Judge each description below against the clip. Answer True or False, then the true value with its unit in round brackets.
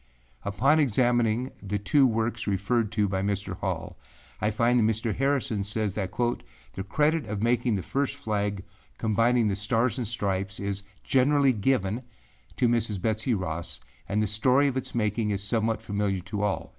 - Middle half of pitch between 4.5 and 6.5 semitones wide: False (3.2 semitones)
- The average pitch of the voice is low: True (110 Hz)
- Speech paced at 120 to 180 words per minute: True (170 wpm)